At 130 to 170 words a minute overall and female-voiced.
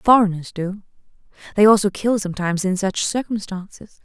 Yes: slow, 135 wpm; female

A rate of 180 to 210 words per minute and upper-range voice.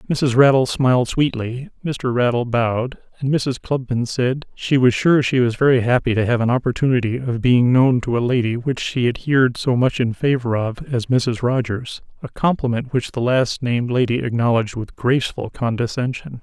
No: average, 185 wpm; low, 125 Hz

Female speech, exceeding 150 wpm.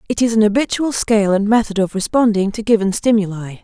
Yes: female; average, 200 wpm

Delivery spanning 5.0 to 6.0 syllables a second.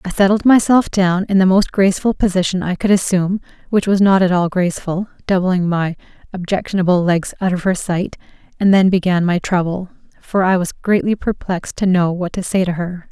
Yes: 5.6 syllables/s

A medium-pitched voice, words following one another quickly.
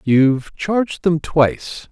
No: medium, 155 Hz; slow, 125 wpm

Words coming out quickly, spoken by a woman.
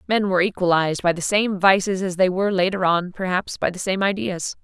Yes: fast, 220 wpm; female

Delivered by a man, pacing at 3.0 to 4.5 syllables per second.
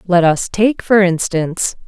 No: female; 4.2 syllables/s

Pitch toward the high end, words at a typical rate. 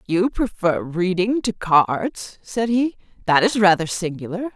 Yes: high, 200 Hz; average, 160 wpm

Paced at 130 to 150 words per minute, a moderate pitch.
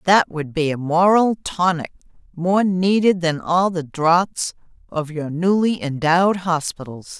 Yes: average, 140 wpm; medium, 170 Hz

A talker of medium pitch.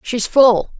No: high, 230 Hz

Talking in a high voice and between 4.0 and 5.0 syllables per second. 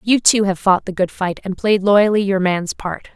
Yes: high, 195 Hz; 4.6 syllables/s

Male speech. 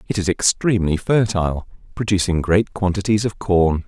Yes: male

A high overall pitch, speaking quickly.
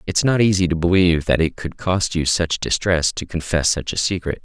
No: very low, 85 Hz; fast, 230 wpm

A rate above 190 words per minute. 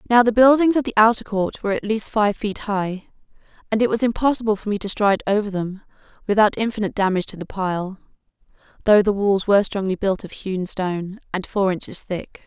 Yes: average, 200 wpm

